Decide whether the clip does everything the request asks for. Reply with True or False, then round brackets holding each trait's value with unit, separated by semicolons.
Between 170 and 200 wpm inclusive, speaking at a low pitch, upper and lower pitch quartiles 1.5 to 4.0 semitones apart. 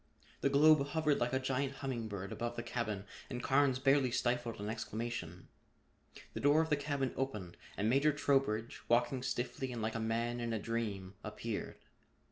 True (175 wpm; 120 Hz; 3.5 semitones)